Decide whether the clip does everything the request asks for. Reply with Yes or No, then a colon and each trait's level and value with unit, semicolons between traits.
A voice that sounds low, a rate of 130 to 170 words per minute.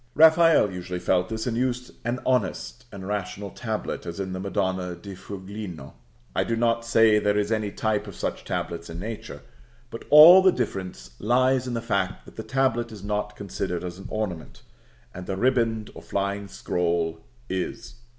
No: low, 105 Hz; average, 180 wpm